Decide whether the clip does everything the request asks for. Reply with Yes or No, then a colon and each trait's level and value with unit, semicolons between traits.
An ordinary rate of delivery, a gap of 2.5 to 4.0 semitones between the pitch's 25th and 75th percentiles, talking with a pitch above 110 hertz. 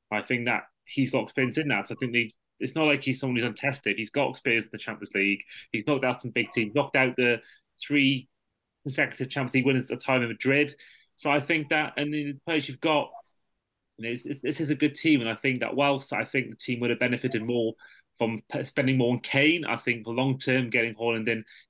No: fast, 240 wpm; average, 3.3 semitones; low, 130 Hz